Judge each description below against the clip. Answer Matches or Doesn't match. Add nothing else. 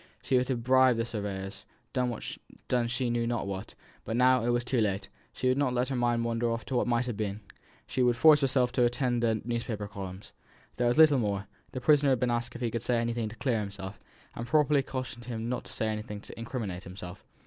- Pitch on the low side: Matches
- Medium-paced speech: Doesn't match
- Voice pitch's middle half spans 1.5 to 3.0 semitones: Matches